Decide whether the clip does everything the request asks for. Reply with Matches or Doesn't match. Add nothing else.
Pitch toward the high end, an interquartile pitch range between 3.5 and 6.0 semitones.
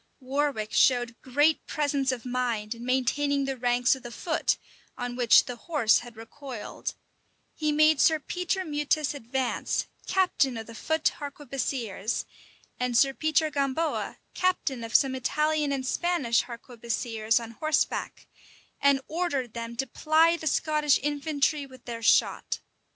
Matches